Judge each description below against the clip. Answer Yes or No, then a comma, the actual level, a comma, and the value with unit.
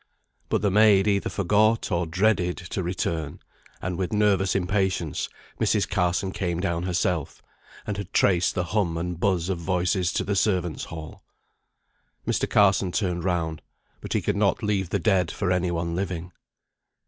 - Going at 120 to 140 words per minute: No, average, 160 wpm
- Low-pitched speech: Yes, very low, 90 Hz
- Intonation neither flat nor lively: No, narrow, 2.3 semitones